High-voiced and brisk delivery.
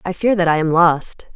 No: medium, 175 Hz; fast, 265 wpm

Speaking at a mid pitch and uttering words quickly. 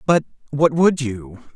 No: medium, 145 Hz; average, 155 wpm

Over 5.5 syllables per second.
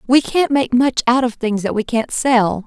No: 4.7 syllables/s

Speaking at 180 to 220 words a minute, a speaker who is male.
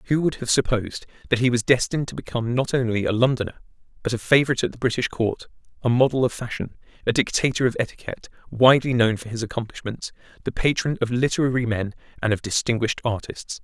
Yes: average, 190 wpm; male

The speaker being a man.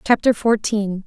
No: female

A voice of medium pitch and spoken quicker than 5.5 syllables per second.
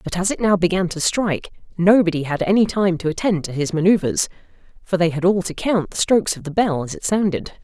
Yes: medium, 180 Hz; 5.9 syllables/s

